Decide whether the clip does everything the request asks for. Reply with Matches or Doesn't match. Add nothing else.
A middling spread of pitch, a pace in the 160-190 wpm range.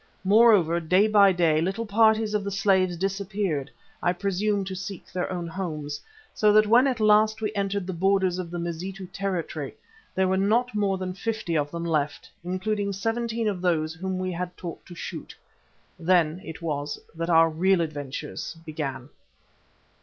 Matches